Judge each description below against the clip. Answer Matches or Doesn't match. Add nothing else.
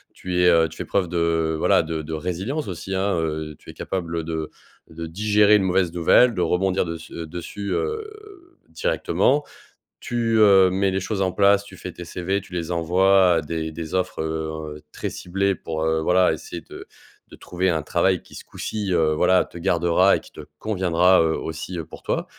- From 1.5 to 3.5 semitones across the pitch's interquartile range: Matches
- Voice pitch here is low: Matches